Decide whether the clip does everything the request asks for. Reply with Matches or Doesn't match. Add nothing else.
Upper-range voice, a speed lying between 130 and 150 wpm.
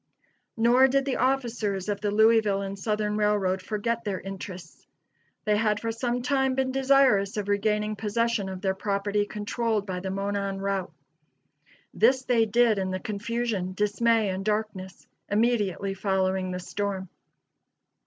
Matches